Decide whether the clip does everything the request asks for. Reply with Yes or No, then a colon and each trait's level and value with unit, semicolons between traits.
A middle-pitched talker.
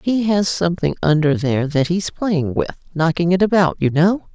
Yes: medium, 170 Hz